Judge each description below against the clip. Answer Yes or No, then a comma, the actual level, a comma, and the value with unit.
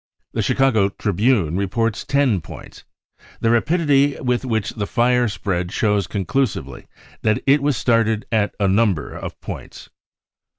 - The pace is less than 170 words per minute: Yes, average, 140 wpm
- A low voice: Yes, low, 110 Hz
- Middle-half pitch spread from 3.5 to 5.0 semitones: Yes, average, 4.2 semitones